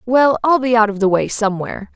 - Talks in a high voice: Yes, high, 225 Hz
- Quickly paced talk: Yes, fast, 245 wpm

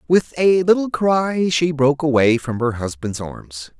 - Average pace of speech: Yes, average, 175 wpm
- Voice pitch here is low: No, medium, 145 Hz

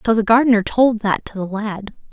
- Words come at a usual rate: No, fast, 225 wpm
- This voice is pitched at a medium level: No, high, 215 Hz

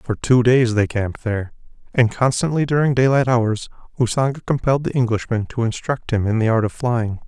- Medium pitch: No, low, 120 Hz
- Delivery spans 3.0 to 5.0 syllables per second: No, 5.5 syllables/s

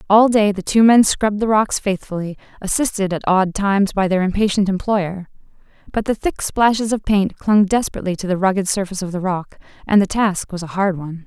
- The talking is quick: Yes, fast, 210 wpm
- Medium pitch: No, high, 195 Hz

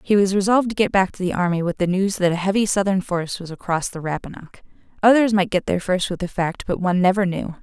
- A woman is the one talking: Yes, female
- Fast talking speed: Yes, fast, 260 wpm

